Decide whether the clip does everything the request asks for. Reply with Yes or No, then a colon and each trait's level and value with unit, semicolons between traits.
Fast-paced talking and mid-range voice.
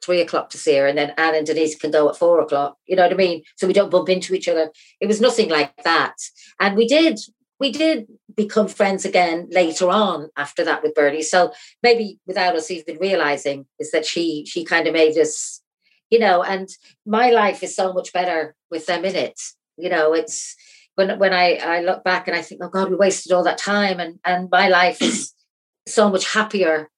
Yes: fast, 220 wpm; medium, 180 Hz